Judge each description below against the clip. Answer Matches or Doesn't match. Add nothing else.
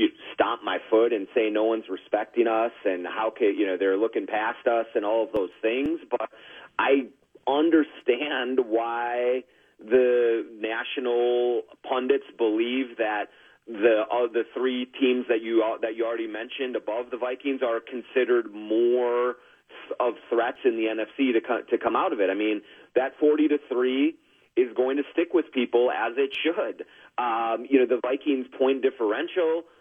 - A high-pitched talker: Doesn't match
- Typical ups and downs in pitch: Matches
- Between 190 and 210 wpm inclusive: Doesn't match